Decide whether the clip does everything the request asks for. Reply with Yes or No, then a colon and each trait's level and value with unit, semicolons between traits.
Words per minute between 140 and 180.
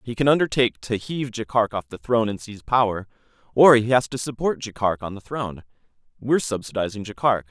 No: average, 190 wpm